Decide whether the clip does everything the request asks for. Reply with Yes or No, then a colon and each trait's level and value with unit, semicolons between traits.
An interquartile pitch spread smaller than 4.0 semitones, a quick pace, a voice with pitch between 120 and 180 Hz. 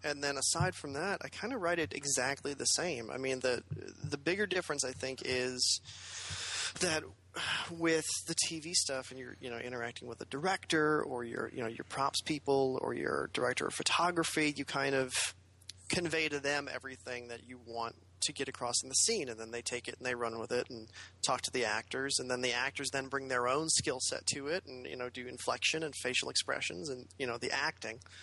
Yes: average, 3.5 semitones; fast, 220 wpm; low, 130 Hz